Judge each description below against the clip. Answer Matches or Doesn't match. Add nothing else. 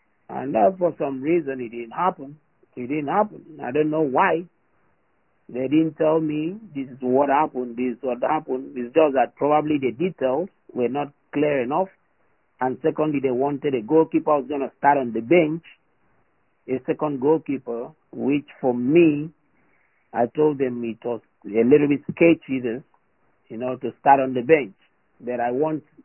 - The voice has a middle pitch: Matches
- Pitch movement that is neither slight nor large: Matches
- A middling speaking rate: Matches